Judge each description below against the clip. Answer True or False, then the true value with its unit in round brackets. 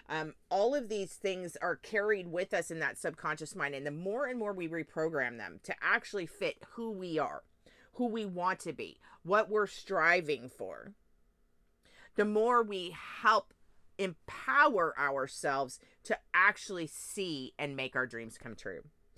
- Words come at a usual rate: True (160 wpm)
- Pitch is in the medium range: True (170 Hz)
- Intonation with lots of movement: True (6.6 semitones)